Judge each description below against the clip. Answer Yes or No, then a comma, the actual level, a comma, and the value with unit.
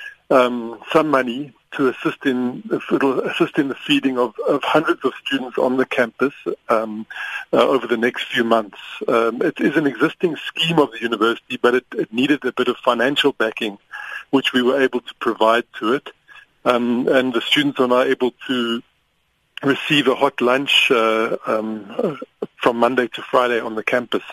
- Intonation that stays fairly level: Yes, narrow, 2.3 semitones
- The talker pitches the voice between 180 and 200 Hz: No, low, 125 Hz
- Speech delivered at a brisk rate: No, average, 180 wpm